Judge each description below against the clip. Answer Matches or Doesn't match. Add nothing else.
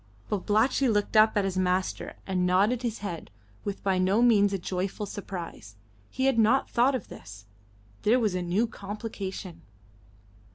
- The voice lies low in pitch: Doesn't match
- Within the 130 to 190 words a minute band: Matches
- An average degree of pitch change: Matches